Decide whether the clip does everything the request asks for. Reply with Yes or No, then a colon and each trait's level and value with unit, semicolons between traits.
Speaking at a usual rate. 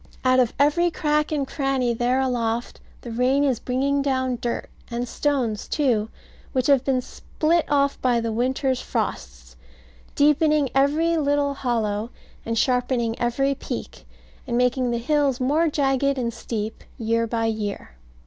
Yes: average, 150 wpm